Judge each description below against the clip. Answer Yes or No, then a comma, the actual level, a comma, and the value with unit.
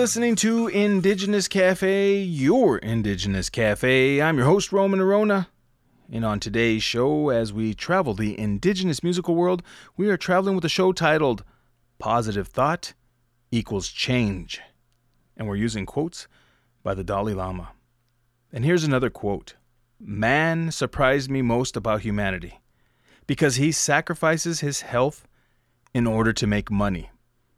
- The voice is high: No, low, 125 Hz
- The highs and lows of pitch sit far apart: Yes, wide, 7.7 semitones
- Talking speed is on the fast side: No, slow, 135 wpm